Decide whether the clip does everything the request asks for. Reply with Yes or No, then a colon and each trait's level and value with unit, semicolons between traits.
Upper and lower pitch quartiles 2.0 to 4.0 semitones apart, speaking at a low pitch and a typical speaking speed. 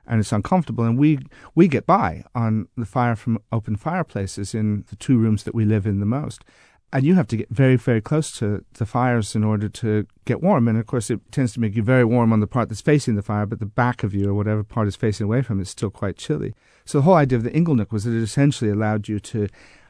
No: average, 2.7 semitones; low, 115 Hz; fast, 260 wpm